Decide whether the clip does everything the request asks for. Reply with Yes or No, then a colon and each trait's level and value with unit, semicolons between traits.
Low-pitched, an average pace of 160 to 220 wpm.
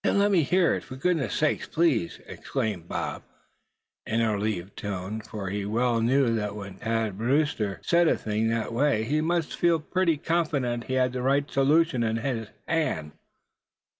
Yes: low, 120 Hz; average, 175 wpm